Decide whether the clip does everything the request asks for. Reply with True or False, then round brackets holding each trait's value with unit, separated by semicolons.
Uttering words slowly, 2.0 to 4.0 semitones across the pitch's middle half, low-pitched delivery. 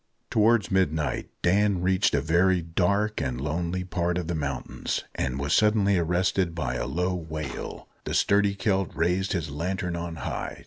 False (165 wpm; 3.1 semitones; 90 Hz)